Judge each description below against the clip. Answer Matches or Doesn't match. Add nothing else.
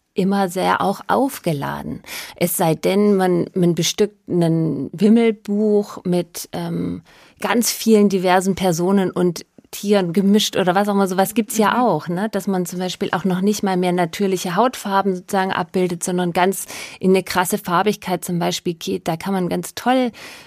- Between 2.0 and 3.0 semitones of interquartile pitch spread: Matches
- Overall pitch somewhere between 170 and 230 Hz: Matches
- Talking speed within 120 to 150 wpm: Doesn't match